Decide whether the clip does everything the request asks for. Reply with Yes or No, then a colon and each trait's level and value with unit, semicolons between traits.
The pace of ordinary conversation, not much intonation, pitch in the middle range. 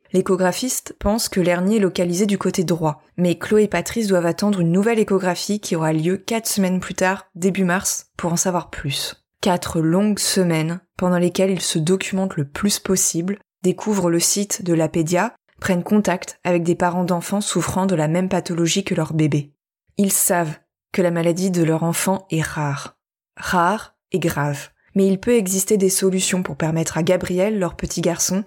Yes: average, 185 wpm; narrow, 2.1 semitones; medium, 180 Hz